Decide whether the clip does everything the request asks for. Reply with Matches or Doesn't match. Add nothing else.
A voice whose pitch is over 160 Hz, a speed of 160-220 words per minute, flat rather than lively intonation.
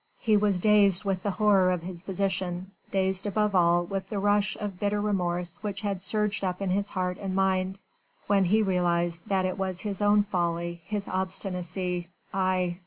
Matches